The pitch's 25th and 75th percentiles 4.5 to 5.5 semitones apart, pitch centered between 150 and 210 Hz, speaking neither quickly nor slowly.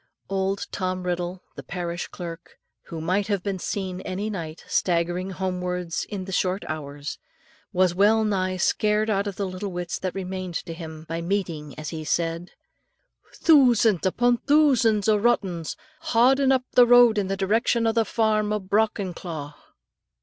No: average, 3.4 semitones; high, 190 Hz; average, 160 wpm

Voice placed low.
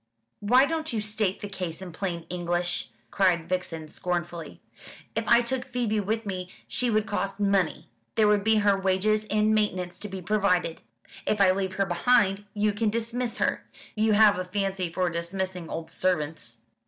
No: high, 195 Hz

